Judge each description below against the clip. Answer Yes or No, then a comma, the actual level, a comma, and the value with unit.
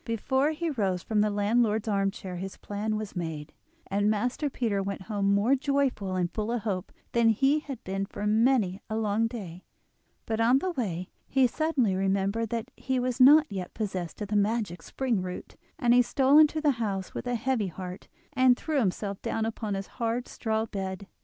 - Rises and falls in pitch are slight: No, average, 4.1 semitones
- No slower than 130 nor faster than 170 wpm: No, average, 195 wpm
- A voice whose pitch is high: Yes, high, 220 Hz